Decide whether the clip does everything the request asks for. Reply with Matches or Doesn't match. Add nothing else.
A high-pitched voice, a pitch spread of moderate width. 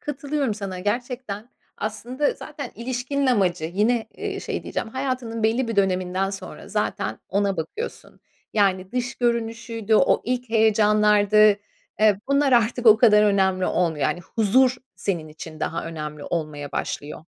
Matches